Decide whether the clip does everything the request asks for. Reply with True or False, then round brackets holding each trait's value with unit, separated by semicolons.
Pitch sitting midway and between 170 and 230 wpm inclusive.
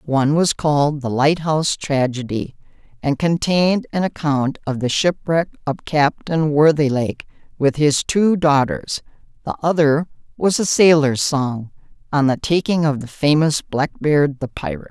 False (150 Hz; 145 wpm)